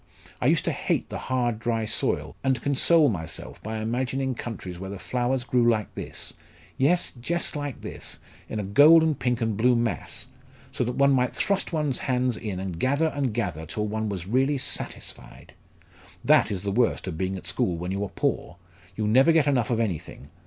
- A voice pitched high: No, low, 120 Hz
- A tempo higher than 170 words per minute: Yes, average, 195 wpm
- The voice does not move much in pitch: No, average, 4.7 semitones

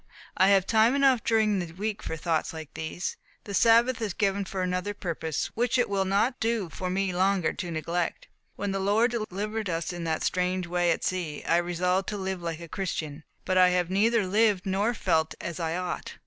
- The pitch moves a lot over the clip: No, average, 3.2 semitones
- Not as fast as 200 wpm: No, fast, 205 wpm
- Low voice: No, high, 190 Hz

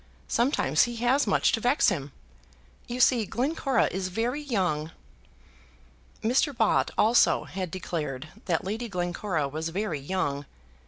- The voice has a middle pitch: No, high, 195 Hz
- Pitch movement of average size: No, wide, 6.8 semitones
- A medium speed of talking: No, slow, 130 wpm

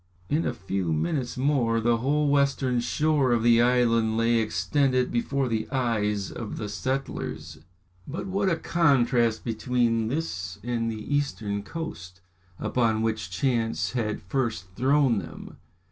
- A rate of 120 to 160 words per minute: Yes, average, 140 wpm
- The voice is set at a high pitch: No, low, 120 Hz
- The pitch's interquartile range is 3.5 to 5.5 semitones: Yes, average, 3.8 semitones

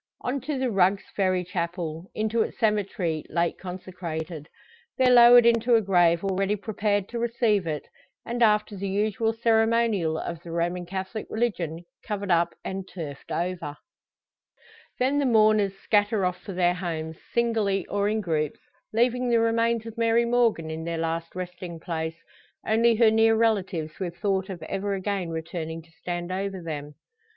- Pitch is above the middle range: Yes, high, 195 Hz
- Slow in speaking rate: No, average, 160 wpm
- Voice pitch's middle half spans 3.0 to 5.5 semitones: Yes, average, 4.6 semitones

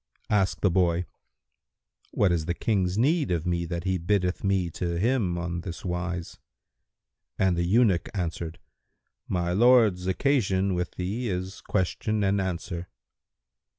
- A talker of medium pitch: No, very low, 90 Hz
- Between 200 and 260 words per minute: No, average, 140 wpm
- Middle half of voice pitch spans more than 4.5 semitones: No, narrow, 2.5 semitones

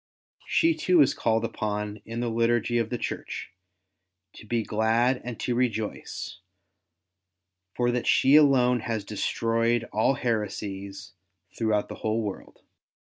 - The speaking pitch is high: No, low, 115 Hz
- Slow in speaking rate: Yes, slow, 130 wpm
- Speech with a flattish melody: Yes, narrow, 2.2 semitones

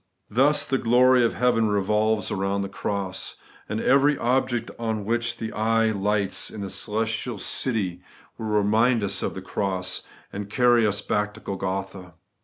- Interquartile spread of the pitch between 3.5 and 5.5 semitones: No, average, 2.9 semitones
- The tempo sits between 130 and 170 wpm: Yes, average, 160 wpm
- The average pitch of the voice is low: Yes, low, 110 Hz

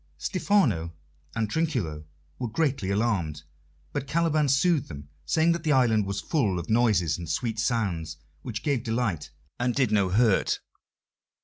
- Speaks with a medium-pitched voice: No, low, 115 Hz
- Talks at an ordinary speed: Yes, average, 145 wpm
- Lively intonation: Yes, wide, 6.7 semitones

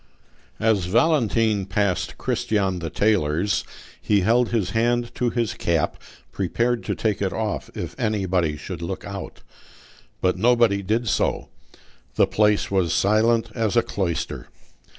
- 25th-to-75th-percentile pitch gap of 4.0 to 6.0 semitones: No, average, 3.5 semitones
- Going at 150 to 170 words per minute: No, slow, 135 wpm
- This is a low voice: Yes, low, 105 Hz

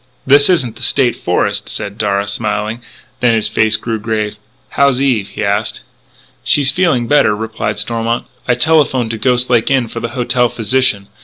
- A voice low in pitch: Yes, low, 115 Hz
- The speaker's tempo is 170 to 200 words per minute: Yes, average, 175 wpm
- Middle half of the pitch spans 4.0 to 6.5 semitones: No, average, 3.3 semitones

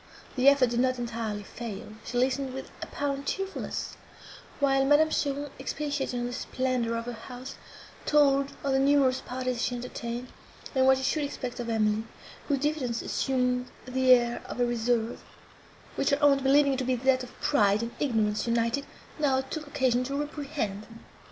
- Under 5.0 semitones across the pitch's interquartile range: Yes, average, 2.7 semitones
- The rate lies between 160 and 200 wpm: Yes, average, 170 wpm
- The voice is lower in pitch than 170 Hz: No, very high, 255 Hz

